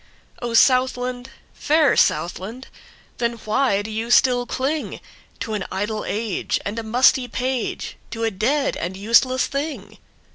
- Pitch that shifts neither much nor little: Yes, average, 3.2 semitones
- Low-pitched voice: No, high, 240 Hz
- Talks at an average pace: No, slow, 120 wpm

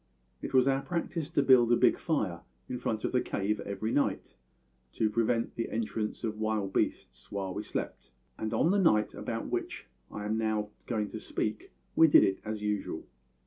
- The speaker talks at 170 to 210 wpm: Yes, average, 190 wpm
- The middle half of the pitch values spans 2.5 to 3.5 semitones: Yes, average, 3.1 semitones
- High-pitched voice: No, low, 110 Hz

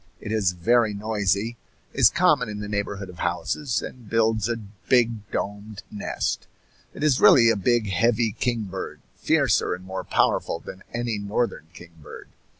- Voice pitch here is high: No, low, 105 Hz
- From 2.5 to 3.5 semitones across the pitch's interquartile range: Yes, average, 2.9 semitones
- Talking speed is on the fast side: No, average, 150 wpm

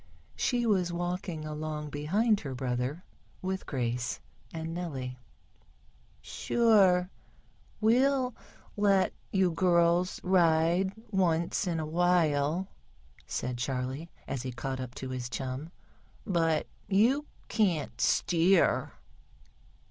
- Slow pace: Yes, slow, 100 wpm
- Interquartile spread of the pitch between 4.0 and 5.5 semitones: Yes, average, 5.1 semitones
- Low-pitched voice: No, medium, 170 Hz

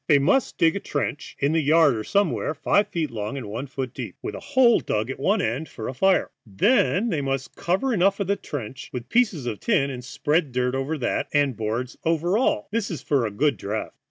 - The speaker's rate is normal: No, fast, 225 wpm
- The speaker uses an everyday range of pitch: No, wide, 6.6 semitones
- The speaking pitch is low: No, medium, 145 Hz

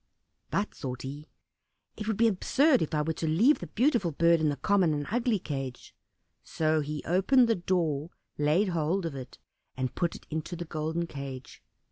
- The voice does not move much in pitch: No, average, 4.7 semitones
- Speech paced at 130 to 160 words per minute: No, average, 185 wpm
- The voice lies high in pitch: No, medium, 165 Hz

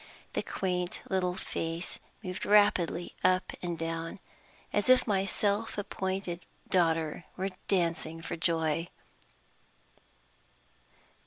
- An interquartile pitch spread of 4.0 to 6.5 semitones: No, narrow, 2.6 semitones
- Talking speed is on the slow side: Yes, slow, 100 wpm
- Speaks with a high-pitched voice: No, medium, 180 Hz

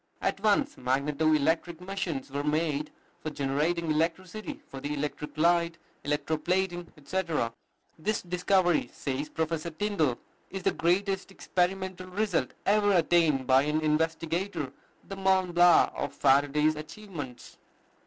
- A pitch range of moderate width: Yes, average, 3.9 semitones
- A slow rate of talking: Yes, slow, 125 wpm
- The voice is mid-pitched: Yes, medium, 165 Hz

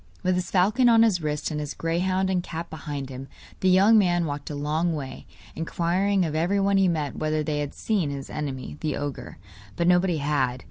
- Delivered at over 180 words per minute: Yes, average, 200 wpm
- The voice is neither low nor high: Yes, medium, 165 Hz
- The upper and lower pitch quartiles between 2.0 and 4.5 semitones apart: Yes, average, 4.0 semitones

